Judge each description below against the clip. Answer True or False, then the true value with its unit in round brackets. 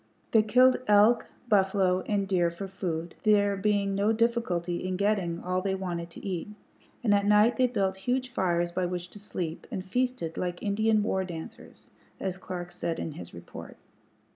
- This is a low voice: False (190 Hz)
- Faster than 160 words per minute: True (175 wpm)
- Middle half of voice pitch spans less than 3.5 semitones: True (3.0 semitones)